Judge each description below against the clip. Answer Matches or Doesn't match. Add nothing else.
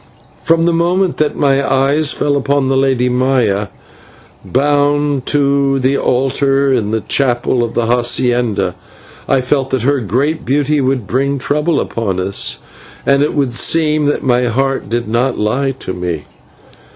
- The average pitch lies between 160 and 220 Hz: Doesn't match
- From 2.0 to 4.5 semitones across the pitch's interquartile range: Matches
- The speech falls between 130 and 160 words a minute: Matches